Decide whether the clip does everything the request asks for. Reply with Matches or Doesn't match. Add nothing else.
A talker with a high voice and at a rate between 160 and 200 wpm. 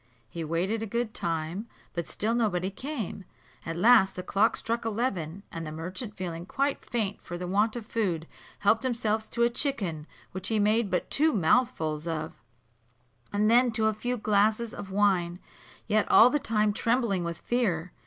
Matches